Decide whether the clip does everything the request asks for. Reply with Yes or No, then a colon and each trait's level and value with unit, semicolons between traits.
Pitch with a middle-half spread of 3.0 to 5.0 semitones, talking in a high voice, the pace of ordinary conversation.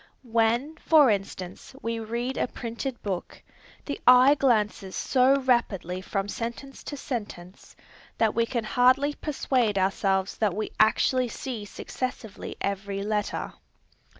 No: average, 4.1 semitones; high, 230 Hz; slow, 125 wpm